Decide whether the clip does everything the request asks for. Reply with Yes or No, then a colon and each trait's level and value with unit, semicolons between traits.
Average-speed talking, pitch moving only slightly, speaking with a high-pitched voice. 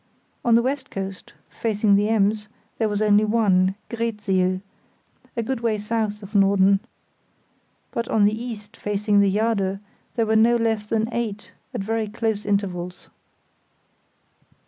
Yes: average, 145 wpm; narrow, 2.0 semitones; high, 210 Hz